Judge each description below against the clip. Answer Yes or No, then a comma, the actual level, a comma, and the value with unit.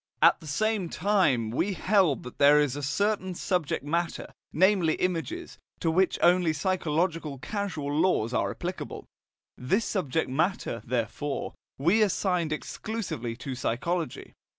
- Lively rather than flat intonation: No, average, 4.8 semitones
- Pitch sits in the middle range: Yes, medium, 165 Hz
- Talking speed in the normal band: No, slow, 130 wpm